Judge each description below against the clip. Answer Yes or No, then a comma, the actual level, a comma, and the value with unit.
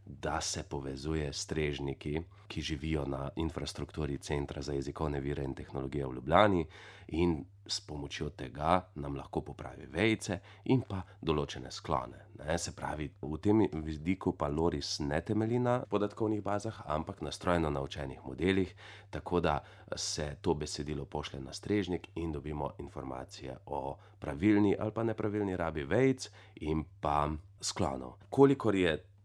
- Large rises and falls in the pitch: Yes, wide, 5.8 semitones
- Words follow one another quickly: No, average, 140 wpm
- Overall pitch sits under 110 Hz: Yes, very low, 80 Hz